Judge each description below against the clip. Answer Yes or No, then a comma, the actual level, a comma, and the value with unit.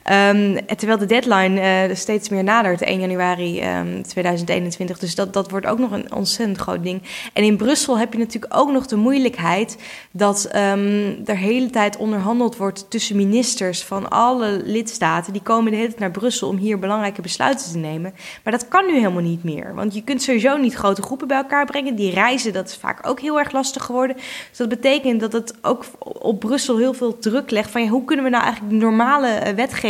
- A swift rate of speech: Yes, fast, 210 wpm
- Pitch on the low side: No, high, 215 Hz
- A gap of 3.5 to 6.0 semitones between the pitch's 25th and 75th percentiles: Yes, average, 3.9 semitones